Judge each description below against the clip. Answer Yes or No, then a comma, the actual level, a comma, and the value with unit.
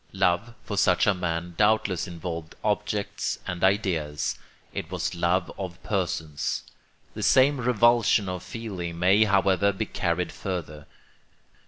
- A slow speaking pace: Yes, slow, 130 wpm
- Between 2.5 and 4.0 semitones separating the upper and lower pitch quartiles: Yes, average, 3.3 semitones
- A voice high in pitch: No, very low, 95 Hz